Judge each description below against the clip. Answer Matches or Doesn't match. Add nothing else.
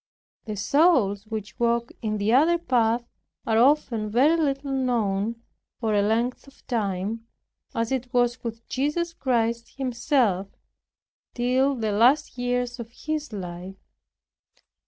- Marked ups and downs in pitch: Doesn't match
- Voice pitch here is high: Matches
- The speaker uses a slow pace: Matches